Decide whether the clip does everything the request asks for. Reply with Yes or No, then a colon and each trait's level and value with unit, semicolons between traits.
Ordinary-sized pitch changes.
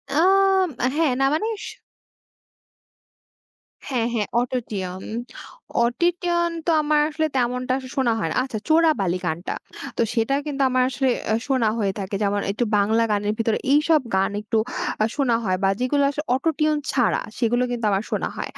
No: wide, 5.9 semitones